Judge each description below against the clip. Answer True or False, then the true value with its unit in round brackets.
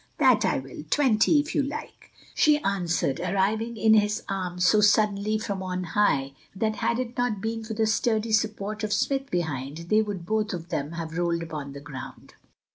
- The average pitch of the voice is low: False (205 Hz)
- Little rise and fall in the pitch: False (4.2 semitones)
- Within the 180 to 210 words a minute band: True (190 wpm)